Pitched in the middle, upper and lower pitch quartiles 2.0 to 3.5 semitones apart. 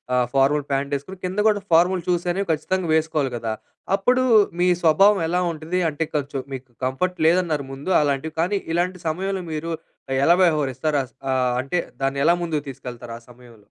No: medium, 155 Hz; average, 4.9 semitones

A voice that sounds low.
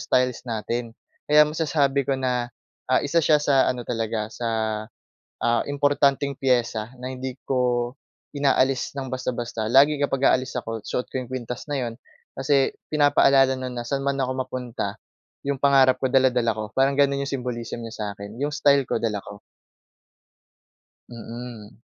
Yes: low, 130 Hz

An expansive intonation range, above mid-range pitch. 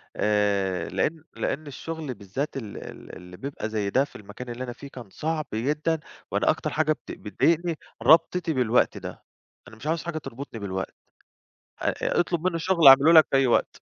No: wide, 6.6 semitones; low, 135 Hz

